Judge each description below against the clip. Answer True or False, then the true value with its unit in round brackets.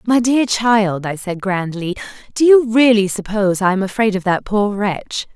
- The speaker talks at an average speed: True (190 wpm)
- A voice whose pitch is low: False (205 Hz)